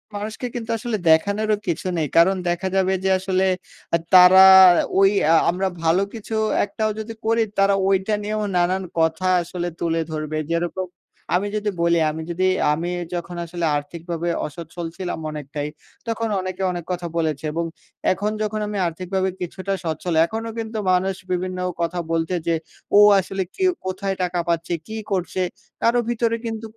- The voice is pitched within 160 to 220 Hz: Yes, medium, 185 Hz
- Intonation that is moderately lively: Yes, average, 3.2 semitones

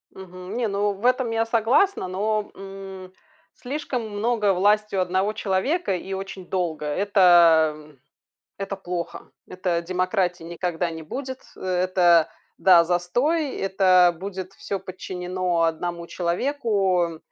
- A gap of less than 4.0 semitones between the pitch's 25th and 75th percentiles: Yes, average, 3.0 semitones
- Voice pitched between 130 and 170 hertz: No, high, 190 Hz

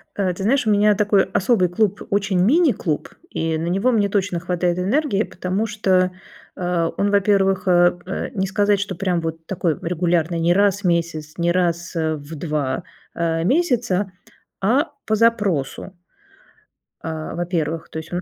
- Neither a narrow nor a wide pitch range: Yes, average, 3.3 semitones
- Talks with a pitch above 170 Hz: Yes, medium, 185 Hz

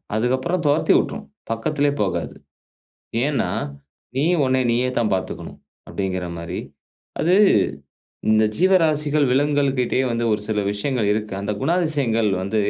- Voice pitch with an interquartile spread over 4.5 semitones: Yes, average, 5.3 semitones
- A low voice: Yes, low, 125 Hz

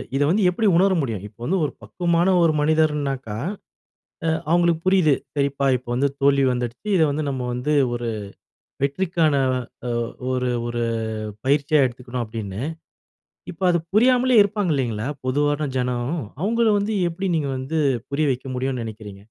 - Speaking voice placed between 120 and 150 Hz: Yes, medium, 140 Hz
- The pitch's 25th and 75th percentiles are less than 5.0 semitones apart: No, wide, 5.5 semitones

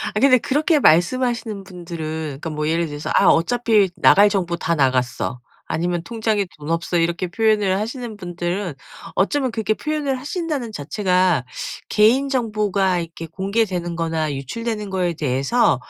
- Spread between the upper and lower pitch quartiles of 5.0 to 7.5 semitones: Yes, average, 5.3 semitones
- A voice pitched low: No, high, 190 Hz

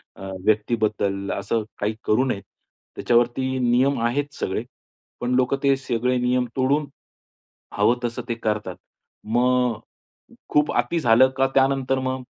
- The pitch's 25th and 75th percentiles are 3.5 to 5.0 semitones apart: No, narrow, 2.5 semitones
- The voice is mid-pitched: No, low, 125 Hz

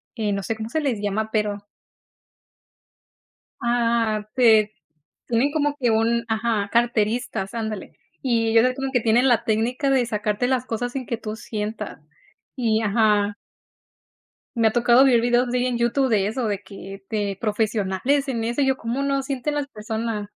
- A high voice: Yes, high, 230 Hz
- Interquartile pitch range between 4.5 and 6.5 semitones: No, average, 2.7 semitones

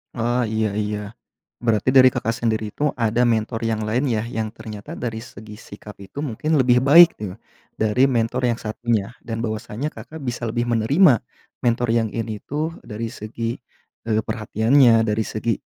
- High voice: No, low, 115 Hz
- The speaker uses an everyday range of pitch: No, narrow, 2.3 semitones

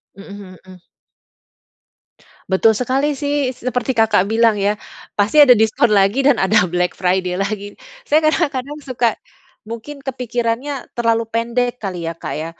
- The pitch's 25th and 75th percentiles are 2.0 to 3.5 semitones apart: No, average, 4.3 semitones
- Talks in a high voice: Yes, high, 230 Hz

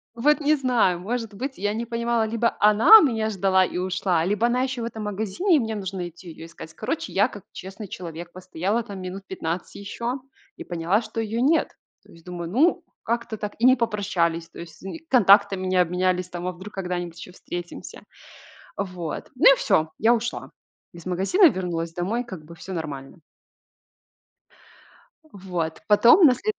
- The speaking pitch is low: No, high, 195 Hz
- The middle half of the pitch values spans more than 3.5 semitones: Yes, average, 4.7 semitones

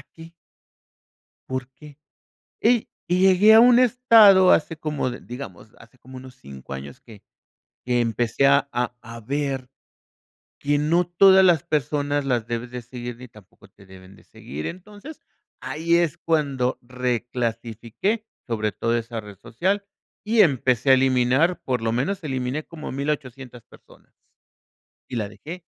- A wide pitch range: Yes, wide, 5.9 semitones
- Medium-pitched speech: No, low, 130 Hz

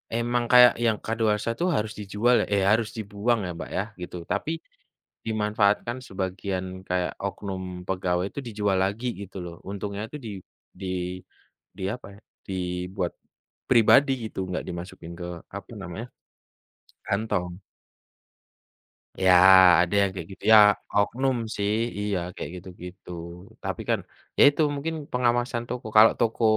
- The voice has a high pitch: No, low, 105 Hz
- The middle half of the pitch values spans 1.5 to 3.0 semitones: No, average, 3.8 semitones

